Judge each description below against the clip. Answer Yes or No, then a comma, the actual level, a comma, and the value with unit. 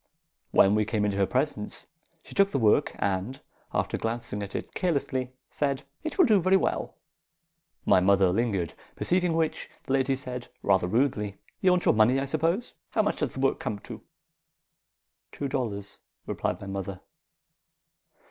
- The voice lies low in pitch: Yes, low, 125 Hz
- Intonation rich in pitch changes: Yes, wide, 6.4 semitones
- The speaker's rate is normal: Yes, average, 165 wpm